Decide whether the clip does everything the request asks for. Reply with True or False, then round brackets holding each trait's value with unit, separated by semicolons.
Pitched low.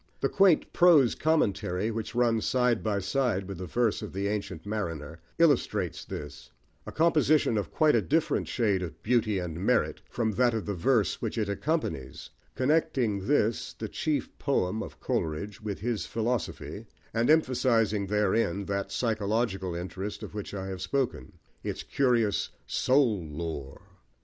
True (110 Hz)